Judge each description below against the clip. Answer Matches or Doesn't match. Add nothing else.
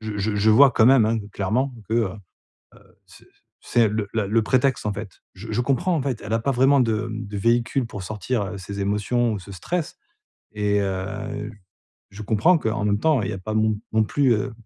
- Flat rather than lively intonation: Doesn't match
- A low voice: Matches